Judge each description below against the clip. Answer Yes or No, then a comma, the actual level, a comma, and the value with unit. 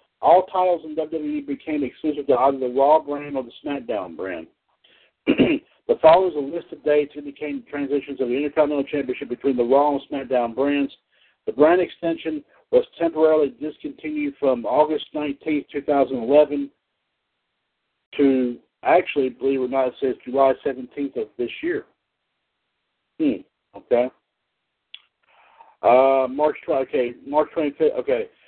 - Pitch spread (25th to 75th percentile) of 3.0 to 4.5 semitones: Yes, average, 3.6 semitones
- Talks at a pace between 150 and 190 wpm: No, average, 140 wpm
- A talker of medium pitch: Yes, medium, 145 Hz